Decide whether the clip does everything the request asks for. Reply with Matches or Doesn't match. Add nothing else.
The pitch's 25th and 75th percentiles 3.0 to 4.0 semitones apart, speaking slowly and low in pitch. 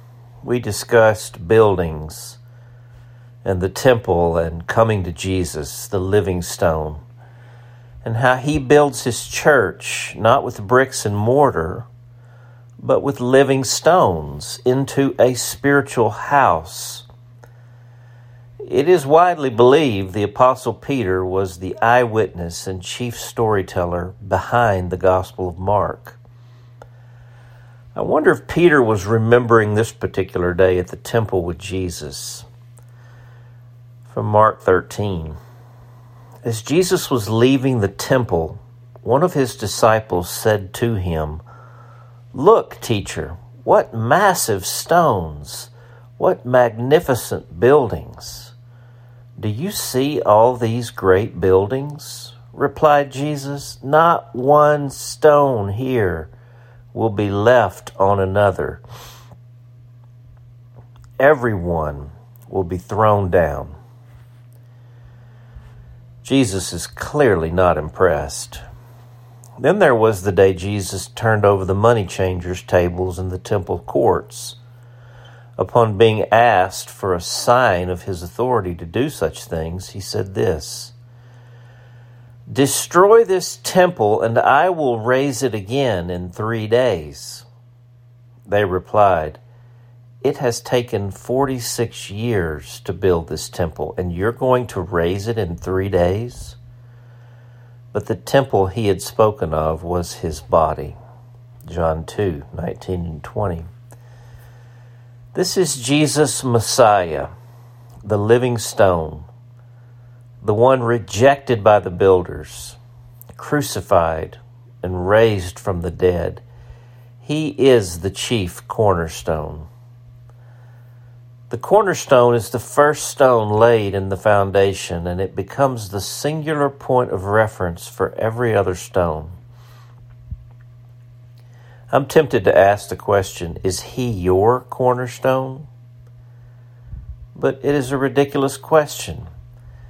Matches